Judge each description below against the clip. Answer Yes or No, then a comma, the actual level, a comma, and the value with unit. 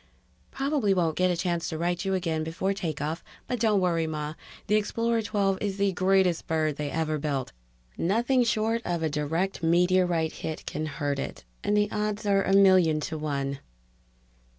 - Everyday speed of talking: Yes, average, 190 wpm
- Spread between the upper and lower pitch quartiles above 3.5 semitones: Yes, average, 4.1 semitones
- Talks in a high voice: No, medium, 180 Hz